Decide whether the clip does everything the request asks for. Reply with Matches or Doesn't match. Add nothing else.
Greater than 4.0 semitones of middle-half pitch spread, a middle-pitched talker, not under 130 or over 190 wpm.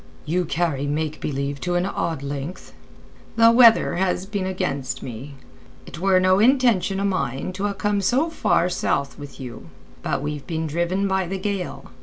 Matches